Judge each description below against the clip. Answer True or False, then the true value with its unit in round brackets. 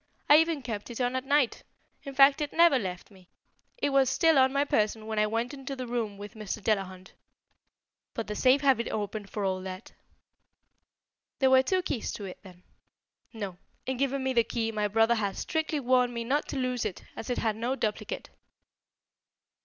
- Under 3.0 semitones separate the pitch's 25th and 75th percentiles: False (4.3 semitones)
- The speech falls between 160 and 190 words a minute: False (200 wpm)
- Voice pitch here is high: True (235 Hz)